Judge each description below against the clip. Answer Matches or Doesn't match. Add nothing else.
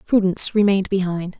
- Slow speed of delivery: Matches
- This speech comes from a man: Doesn't match